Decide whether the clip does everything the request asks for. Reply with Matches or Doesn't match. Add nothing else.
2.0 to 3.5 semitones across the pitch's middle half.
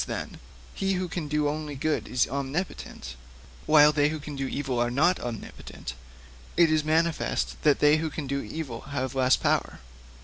Matches